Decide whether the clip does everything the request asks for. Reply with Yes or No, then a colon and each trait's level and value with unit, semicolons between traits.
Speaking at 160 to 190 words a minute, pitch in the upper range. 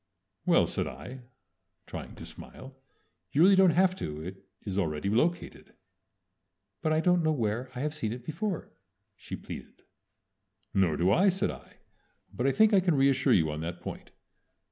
No: average, 170 wpm; low, 130 Hz